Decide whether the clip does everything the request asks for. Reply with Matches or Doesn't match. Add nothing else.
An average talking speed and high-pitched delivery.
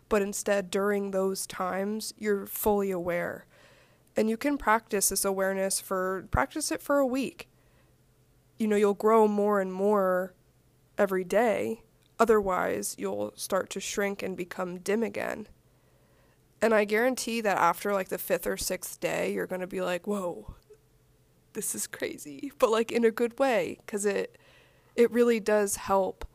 Matches